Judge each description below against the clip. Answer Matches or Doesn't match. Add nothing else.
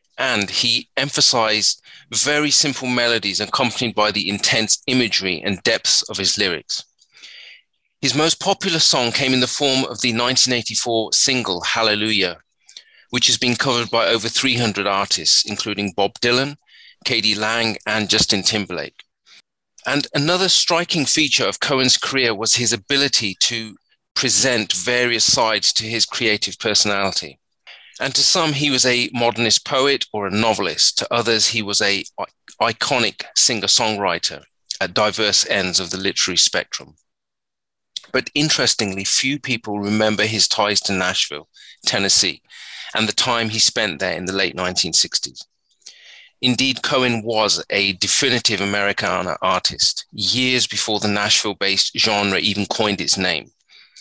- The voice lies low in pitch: Matches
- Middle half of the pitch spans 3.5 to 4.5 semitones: Matches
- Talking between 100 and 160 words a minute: Matches